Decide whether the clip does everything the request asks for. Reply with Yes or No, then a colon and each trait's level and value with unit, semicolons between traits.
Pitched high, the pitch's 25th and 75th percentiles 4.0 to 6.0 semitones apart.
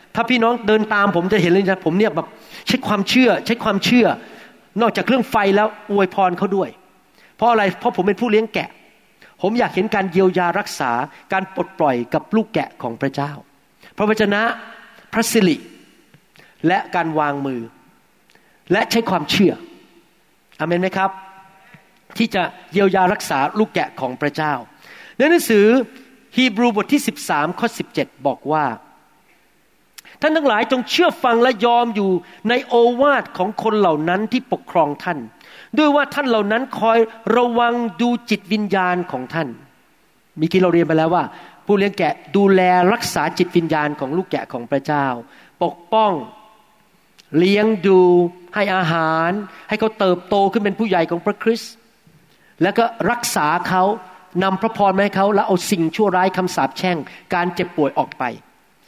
Yes: high, 195 Hz; average, 4.3 semitones